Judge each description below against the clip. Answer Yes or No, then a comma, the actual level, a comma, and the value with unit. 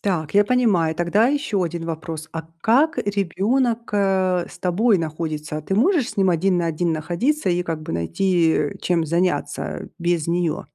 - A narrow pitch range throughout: No, average, 4.0 semitones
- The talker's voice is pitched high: No, medium, 180 Hz